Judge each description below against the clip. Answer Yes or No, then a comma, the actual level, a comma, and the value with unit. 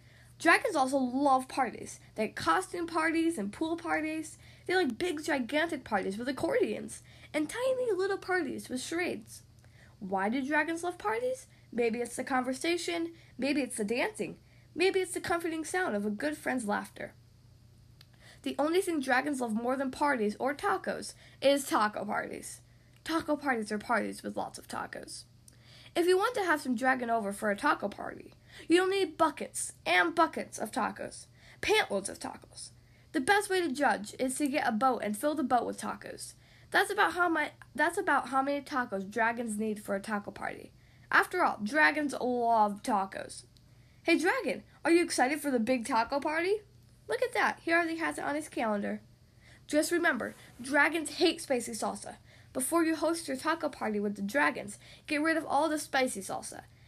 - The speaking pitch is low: No, very high, 280 Hz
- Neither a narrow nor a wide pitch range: No, wide, 6.8 semitones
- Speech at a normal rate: Yes, average, 175 wpm